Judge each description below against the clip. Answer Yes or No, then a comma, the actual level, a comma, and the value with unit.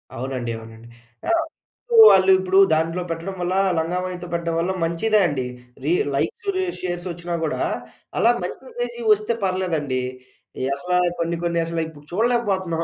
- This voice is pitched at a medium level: Yes, medium, 175 Hz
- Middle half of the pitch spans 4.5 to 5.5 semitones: No, average, 2.8 semitones